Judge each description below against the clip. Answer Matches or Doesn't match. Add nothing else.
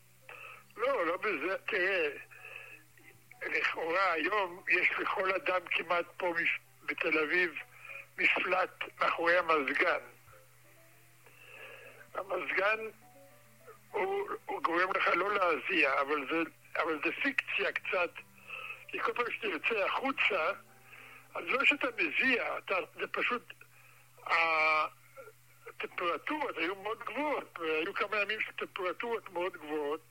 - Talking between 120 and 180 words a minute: Doesn't match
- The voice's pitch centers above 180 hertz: Matches